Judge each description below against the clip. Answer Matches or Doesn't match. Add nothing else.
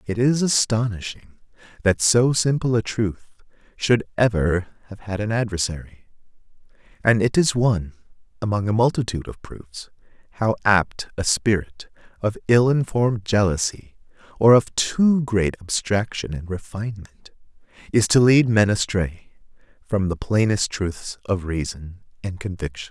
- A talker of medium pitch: Doesn't match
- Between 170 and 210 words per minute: Doesn't match